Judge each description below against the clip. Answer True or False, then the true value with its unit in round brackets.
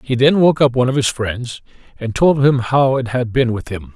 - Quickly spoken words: True (260 wpm)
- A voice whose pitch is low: True (125 Hz)